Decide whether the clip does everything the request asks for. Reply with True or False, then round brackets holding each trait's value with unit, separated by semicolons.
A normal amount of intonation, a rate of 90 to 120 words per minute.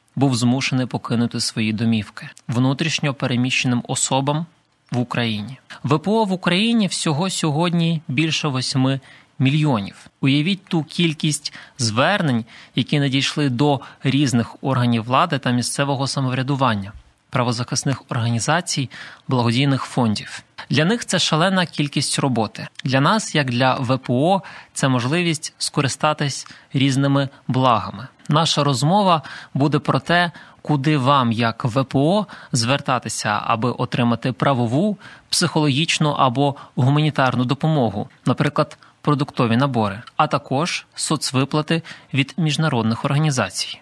True (3.5 semitones; 105 wpm)